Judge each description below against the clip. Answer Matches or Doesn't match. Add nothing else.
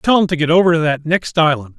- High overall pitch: Doesn't match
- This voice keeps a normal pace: Doesn't match